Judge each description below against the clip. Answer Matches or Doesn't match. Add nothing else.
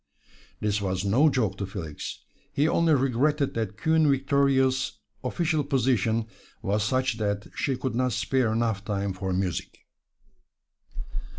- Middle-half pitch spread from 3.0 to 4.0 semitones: Doesn't match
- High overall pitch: Doesn't match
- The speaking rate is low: Matches